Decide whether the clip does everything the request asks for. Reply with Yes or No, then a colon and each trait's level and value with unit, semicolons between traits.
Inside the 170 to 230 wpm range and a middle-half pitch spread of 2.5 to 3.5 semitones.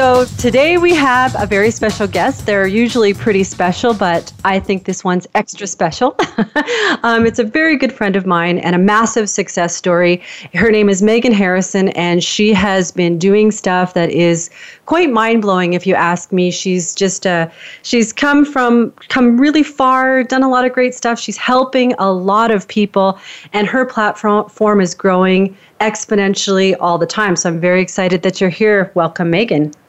No: average, 185 wpm; average, 4.4 semitones